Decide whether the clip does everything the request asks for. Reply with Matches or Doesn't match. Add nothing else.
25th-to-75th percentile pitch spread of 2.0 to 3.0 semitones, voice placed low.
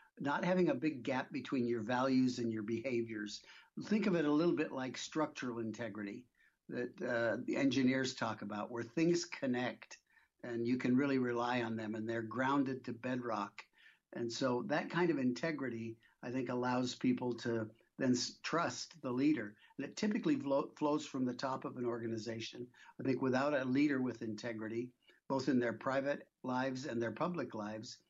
Matches